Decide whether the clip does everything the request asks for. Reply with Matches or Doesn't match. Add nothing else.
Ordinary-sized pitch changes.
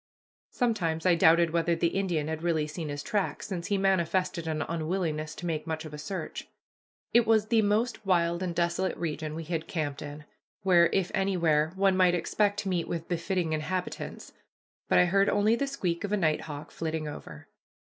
Matches